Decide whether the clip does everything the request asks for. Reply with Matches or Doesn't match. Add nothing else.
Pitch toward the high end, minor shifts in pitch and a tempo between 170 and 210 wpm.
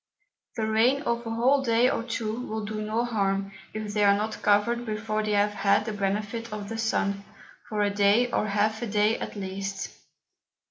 Matches